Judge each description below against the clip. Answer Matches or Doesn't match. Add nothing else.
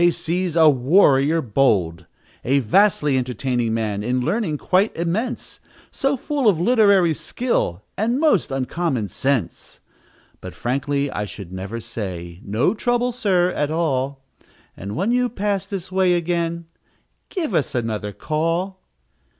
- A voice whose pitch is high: Doesn't match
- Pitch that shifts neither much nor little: Doesn't match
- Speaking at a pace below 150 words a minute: Matches